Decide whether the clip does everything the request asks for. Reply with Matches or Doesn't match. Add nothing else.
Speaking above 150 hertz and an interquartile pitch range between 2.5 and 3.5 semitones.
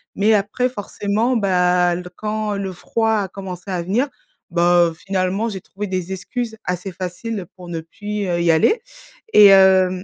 Matches